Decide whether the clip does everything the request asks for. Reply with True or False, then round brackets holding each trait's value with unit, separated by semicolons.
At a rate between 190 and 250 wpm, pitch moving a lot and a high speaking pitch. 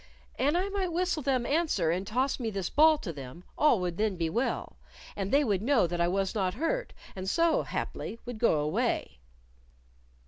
True (195 wpm; 8.6 semitones; 225 Hz)